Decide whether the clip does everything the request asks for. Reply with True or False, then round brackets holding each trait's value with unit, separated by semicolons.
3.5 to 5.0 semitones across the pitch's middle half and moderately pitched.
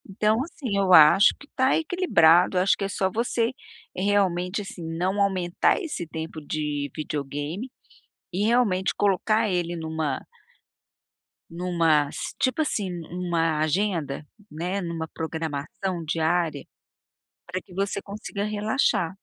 True (4.0 semitones; 180 Hz)